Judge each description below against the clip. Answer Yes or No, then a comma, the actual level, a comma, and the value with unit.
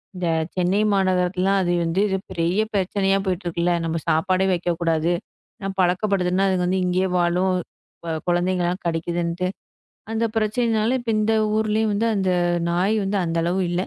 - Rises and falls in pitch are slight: Yes, narrow, 2.1 semitones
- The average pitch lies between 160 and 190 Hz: Yes, medium, 185 Hz